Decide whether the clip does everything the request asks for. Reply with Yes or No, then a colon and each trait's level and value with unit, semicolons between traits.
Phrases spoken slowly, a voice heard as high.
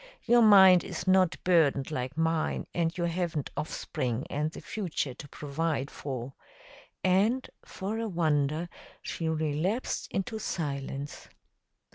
No: slow, 125 wpm; medium, 165 Hz